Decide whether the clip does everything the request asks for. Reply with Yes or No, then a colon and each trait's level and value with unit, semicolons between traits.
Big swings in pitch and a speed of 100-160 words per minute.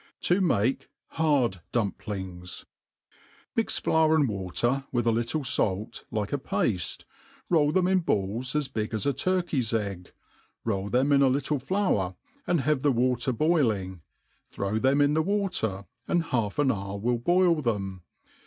Yes: wide, 6.7 semitones; average, 155 wpm